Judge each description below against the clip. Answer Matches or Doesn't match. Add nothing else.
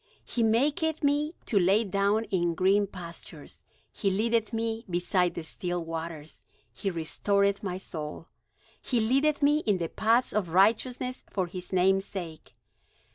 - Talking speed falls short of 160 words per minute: Matches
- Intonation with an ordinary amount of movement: Matches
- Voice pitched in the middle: Doesn't match